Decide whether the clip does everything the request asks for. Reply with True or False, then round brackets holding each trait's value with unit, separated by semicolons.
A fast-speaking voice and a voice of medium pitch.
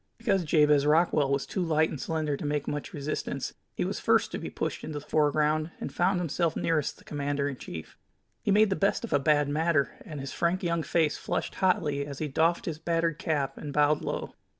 True (220 wpm; 155 Hz)